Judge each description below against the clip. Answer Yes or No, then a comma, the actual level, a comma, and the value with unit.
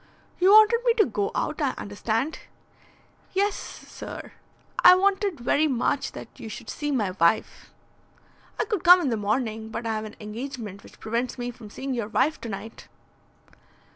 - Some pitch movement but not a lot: No, wide, 7.7 semitones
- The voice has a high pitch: Yes, high, 245 Hz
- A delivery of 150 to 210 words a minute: Yes, average, 170 wpm